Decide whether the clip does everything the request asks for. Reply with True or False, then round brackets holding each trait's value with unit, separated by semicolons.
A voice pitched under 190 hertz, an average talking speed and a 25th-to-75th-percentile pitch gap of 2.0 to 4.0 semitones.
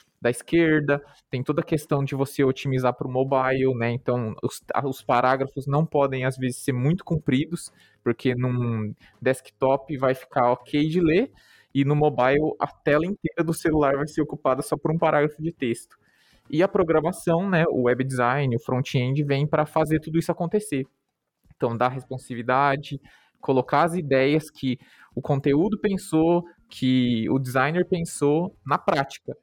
True (140 Hz; 165 wpm; 3.6 semitones)